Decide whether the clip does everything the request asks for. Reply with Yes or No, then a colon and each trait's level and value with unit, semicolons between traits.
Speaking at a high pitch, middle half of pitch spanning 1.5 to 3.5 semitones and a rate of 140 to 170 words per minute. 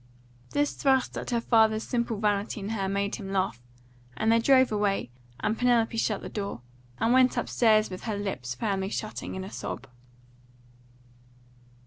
Yes: high, 215 Hz; average, 2.8 semitones; average, 165 wpm